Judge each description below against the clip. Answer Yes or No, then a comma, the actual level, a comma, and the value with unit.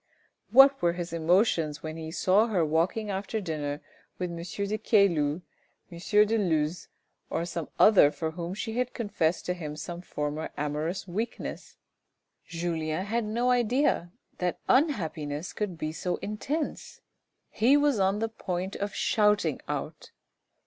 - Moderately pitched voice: Yes, medium, 180 Hz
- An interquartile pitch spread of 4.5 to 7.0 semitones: Yes, average, 4.9 semitones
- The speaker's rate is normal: Yes, average, 145 wpm